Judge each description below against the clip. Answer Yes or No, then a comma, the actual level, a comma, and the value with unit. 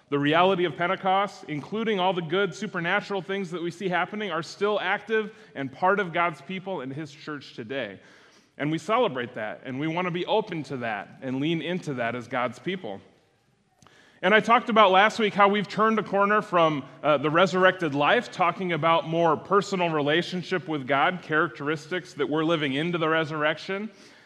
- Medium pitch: Yes, medium, 175 Hz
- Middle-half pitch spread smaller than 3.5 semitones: No, average, 4.3 semitones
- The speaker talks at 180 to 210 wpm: Yes, average, 185 wpm